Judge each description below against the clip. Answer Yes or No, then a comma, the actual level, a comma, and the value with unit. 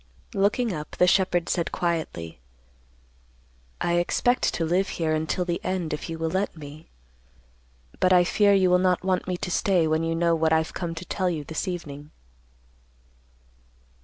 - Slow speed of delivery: No, average, 170 wpm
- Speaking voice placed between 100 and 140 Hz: No, medium, 175 Hz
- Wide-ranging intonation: No, narrow, 2.5 semitones